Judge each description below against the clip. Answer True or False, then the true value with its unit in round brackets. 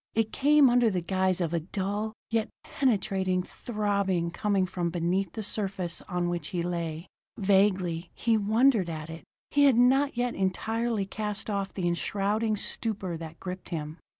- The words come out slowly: False (160 wpm)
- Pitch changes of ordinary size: True (3.9 semitones)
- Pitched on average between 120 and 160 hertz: False (195 Hz)